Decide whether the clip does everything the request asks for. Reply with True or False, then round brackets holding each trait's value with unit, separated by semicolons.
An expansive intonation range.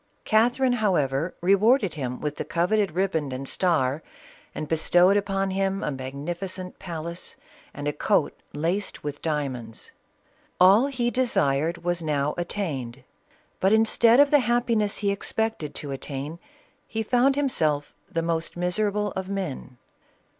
True (5.9 semitones)